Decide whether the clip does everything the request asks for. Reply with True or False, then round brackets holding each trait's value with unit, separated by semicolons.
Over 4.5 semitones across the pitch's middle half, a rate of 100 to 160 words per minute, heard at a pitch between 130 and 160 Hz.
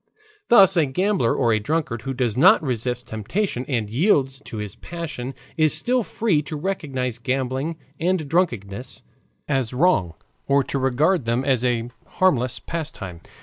True (5.4 semitones; 150 wpm; 135 Hz)